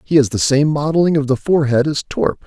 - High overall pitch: No, medium, 145 Hz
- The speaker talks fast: Yes, fast, 245 wpm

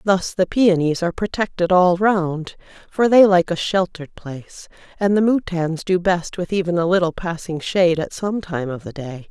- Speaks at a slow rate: No, average, 195 wpm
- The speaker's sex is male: No, female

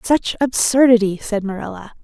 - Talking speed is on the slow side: Yes, slow, 120 wpm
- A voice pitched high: Yes, high, 230 Hz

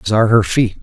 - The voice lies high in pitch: No, low, 110 Hz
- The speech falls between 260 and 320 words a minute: Yes, fast, 290 wpm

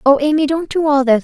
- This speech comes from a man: No, female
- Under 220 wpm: No, fast, 290 wpm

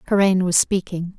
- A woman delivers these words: Yes, female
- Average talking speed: Yes, average, 150 wpm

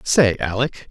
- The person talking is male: Yes, male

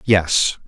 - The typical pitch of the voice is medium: No, very low, 95 Hz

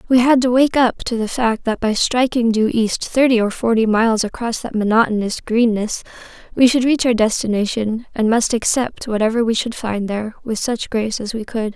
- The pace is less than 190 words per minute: No, fast, 205 wpm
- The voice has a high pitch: Yes, high, 230 Hz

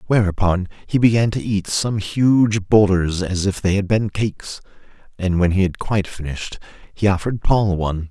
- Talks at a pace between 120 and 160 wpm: No, average, 180 wpm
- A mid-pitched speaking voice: No, low, 100 Hz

